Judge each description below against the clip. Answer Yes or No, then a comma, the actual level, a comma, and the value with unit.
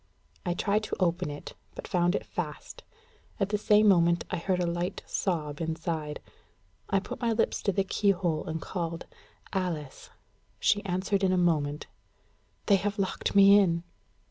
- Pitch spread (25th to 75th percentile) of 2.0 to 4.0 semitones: Yes, average, 3.0 semitones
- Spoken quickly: No, average, 165 wpm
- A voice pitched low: No, medium, 180 Hz